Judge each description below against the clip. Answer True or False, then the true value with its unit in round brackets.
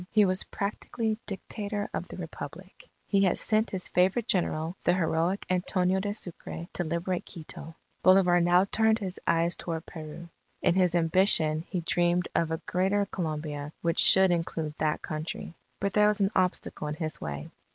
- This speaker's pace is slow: False (170 wpm)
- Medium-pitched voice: True (180 Hz)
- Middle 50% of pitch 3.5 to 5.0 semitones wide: False (3.0 semitones)